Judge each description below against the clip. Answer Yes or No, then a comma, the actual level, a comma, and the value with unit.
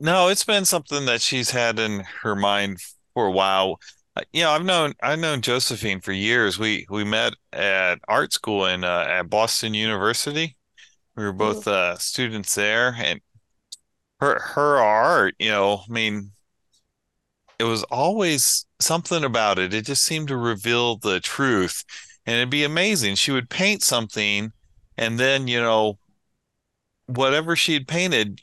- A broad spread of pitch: Yes, wide, 5.8 semitones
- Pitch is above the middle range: No, low, 115 Hz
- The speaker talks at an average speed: Yes, average, 160 wpm